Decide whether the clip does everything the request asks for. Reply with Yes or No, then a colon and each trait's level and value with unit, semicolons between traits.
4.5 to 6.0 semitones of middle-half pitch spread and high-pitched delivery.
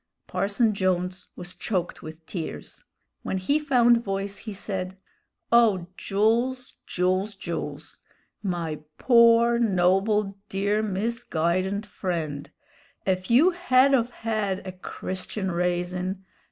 No: average, 4.0 semitones; high, 195 Hz